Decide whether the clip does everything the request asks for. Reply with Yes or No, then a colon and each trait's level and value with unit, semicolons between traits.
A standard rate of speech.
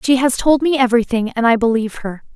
No: fast, 230 wpm